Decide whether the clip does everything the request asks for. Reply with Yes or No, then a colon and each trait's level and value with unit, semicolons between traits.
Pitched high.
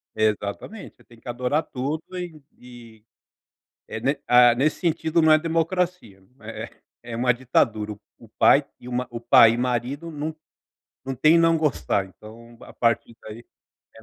No: low, 125 Hz